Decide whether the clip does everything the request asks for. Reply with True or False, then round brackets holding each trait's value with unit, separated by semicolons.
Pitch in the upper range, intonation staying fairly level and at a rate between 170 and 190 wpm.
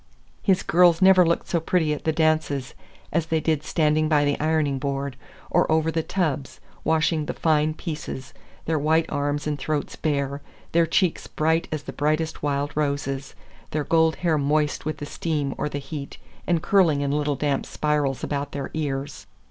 False (150 Hz; 2.1 semitones; 180 wpm)